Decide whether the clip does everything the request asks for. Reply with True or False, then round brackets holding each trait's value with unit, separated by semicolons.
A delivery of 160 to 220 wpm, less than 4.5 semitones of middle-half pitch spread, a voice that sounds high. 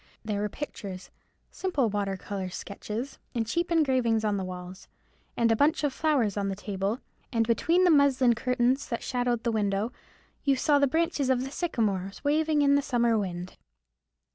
False (165 wpm; 5.6 semitones; 235 Hz)